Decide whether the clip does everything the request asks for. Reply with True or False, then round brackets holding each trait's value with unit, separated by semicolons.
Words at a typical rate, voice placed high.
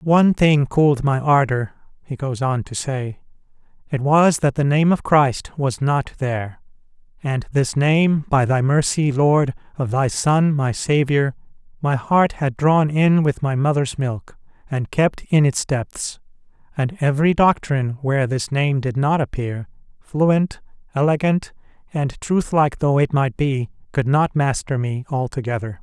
False (160 wpm; 140 Hz)